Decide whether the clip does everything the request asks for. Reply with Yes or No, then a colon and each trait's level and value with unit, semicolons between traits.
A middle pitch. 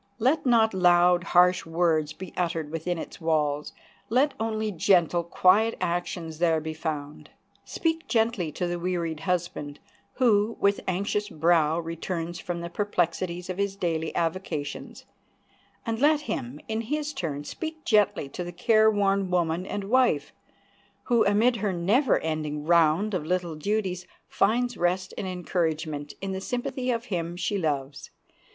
Yes: medium, 180 Hz